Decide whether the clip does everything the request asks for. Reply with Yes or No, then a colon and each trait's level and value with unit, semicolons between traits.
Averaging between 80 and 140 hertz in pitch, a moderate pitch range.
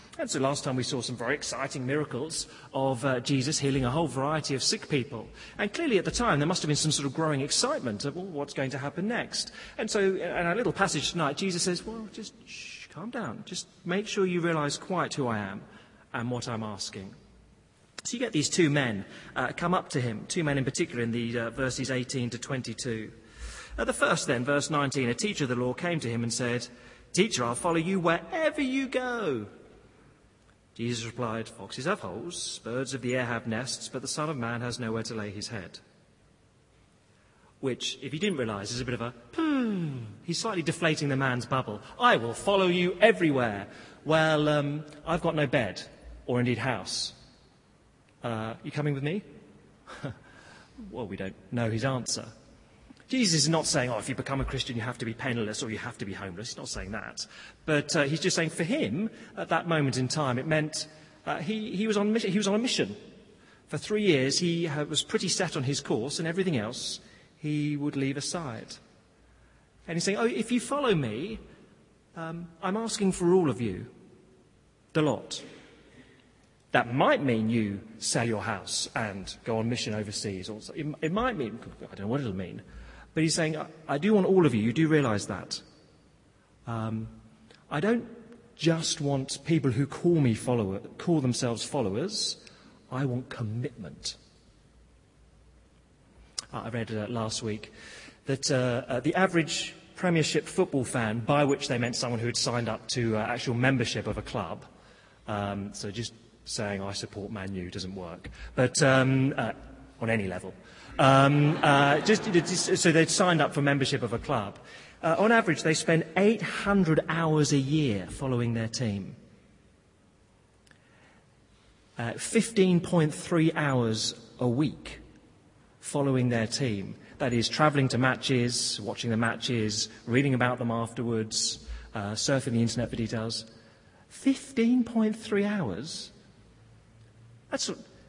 No: low, 135 Hz; wide, 6.0 semitones